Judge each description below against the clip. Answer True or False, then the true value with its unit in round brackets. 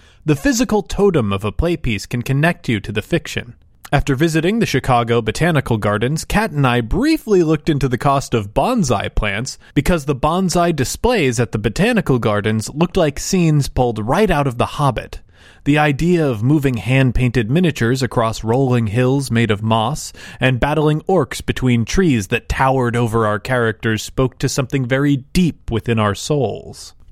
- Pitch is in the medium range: False (130 Hz)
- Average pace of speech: True (170 wpm)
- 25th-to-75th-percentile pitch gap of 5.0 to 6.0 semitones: True (5.4 semitones)